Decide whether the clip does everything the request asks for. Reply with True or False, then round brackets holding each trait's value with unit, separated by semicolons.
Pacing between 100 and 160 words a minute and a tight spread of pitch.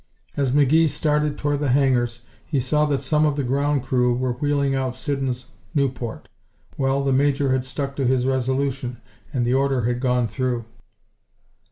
False (170 wpm; 2.2 semitones)